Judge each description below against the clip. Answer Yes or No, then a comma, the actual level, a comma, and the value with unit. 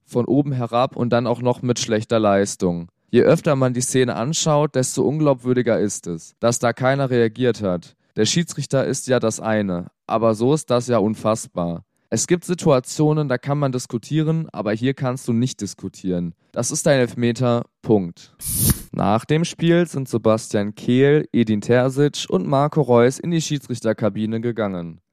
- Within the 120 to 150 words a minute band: No, average, 165 wpm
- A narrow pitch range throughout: No, average, 4.2 semitones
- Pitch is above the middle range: No, low, 120 Hz